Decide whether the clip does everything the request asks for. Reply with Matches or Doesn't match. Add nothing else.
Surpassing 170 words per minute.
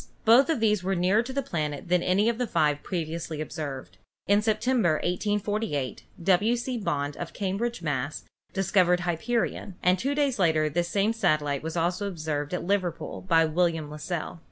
Matches